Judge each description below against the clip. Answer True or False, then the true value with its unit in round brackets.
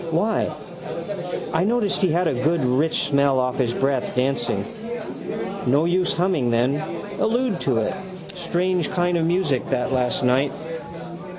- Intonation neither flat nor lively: False (5.7 semitones)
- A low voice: False (150 Hz)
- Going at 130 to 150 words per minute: True (140 wpm)